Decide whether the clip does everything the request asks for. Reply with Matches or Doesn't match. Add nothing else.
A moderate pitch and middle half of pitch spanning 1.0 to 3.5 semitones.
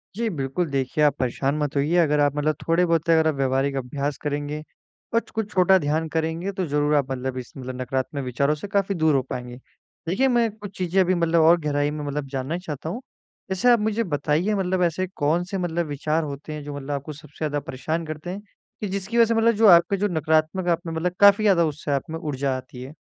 Doesn't match